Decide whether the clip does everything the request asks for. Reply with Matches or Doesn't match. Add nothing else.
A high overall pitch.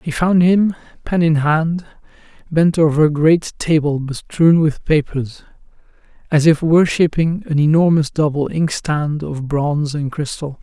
Doesn't match